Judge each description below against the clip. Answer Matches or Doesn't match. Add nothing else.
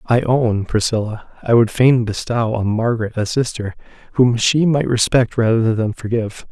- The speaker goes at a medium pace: Matches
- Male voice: Matches